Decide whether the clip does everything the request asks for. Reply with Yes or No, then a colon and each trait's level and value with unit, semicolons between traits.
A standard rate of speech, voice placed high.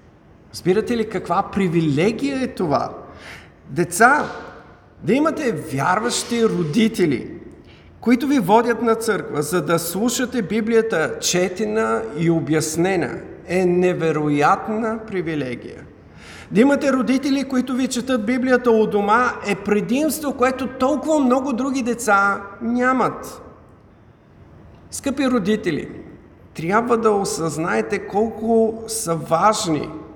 No: slow, 100 wpm; high, 220 Hz